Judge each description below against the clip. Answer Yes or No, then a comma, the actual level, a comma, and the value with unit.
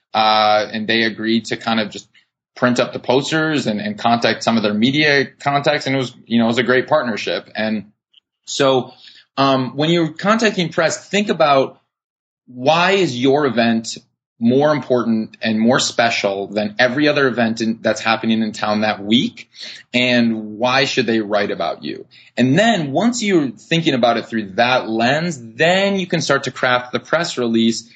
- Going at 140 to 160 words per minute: No, average, 180 wpm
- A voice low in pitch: Yes, low, 125 Hz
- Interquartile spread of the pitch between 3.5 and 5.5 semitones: Yes, average, 4.6 semitones